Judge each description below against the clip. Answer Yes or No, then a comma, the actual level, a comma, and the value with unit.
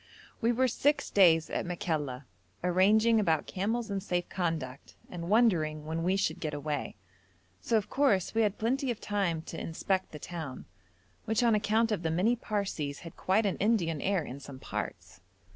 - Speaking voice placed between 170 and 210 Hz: Yes, medium, 185 Hz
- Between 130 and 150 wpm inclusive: No, average, 175 wpm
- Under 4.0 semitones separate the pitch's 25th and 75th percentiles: No, average, 5.2 semitones